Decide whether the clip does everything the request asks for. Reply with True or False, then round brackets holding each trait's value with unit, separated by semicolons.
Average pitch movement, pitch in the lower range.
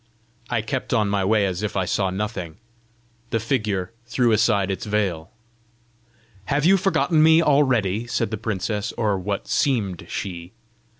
True (3.8 semitones; 105 Hz)